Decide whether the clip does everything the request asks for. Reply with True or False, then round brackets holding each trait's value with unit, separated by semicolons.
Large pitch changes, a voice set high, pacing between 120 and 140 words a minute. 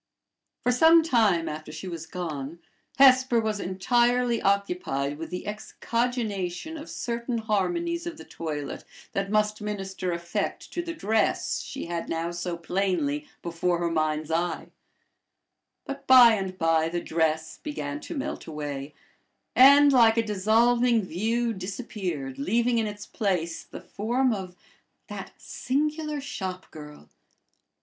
True (6.3 semitones; 200 Hz; 135 wpm)